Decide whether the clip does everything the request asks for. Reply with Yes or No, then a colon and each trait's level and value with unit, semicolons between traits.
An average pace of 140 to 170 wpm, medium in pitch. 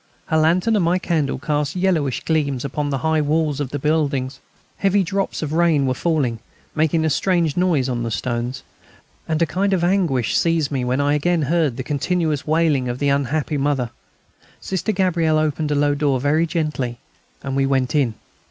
No: average, 190 wpm; medium, 150 Hz